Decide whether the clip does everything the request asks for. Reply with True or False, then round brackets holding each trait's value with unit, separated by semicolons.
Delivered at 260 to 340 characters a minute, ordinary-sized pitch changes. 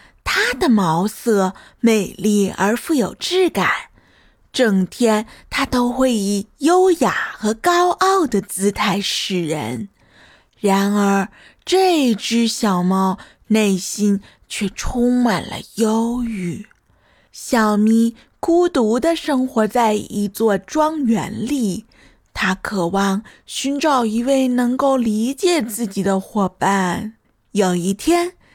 False (155 characters per minute; 4.6 semitones)